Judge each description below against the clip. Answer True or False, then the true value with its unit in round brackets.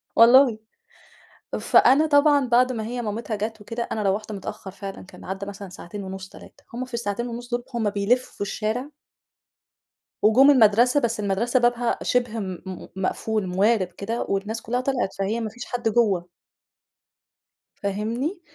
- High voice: True (225 Hz)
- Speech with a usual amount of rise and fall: True (3.3 semitones)